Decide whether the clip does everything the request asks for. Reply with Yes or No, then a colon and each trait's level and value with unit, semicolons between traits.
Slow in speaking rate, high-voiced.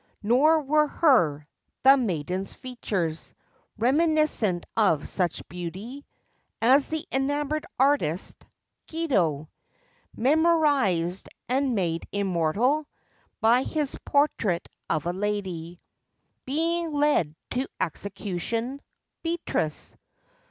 Yes: slow, 80 wpm; high, 235 Hz